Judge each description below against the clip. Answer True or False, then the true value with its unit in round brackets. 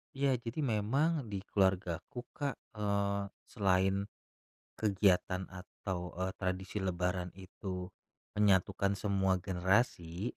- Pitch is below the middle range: True (95 Hz)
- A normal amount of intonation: False (2.3 semitones)